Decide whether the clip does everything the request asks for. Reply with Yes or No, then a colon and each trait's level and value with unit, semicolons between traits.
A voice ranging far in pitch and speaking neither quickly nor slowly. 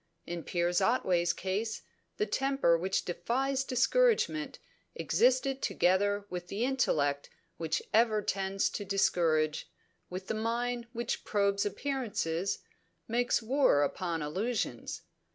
No: wide, 5.7 semitones; slow, 115 wpm